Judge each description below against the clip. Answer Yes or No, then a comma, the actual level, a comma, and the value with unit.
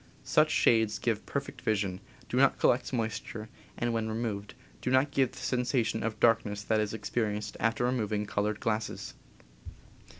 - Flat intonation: Yes, narrow, 2.1 semitones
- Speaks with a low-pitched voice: Yes, low, 110 Hz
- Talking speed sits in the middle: Yes, average, 160 wpm